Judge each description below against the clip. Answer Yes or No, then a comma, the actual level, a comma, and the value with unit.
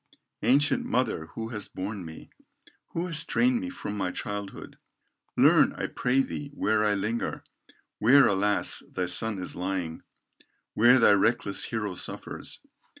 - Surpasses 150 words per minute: No, average, 145 wpm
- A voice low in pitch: Yes, low, 105 Hz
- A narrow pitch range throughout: No, average, 4.5 semitones